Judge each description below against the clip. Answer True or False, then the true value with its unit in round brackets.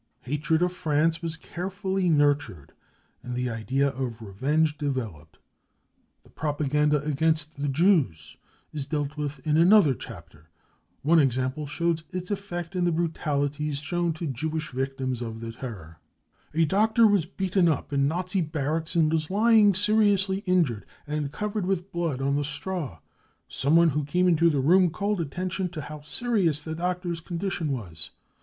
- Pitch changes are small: False (4.3 semitones)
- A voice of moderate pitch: True (155 Hz)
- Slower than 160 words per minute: False (165 wpm)